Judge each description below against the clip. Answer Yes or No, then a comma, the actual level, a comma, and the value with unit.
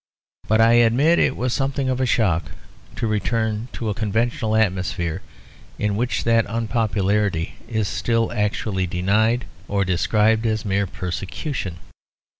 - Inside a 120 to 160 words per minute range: Yes, slow, 135 wpm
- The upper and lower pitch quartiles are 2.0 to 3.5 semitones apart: Yes, average, 2.8 semitones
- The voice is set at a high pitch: No, low, 110 Hz